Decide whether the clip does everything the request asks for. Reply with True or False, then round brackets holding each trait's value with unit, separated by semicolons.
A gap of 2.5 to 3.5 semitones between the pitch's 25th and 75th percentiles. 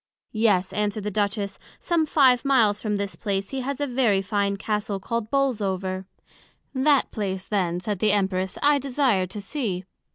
False (4.8 semitones)